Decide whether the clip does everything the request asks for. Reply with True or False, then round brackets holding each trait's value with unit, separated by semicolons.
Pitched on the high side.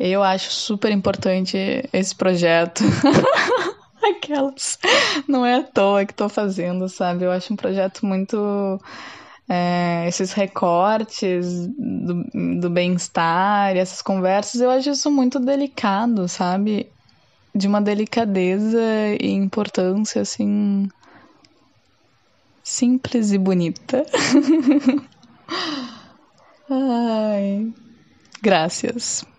True (210 Hz)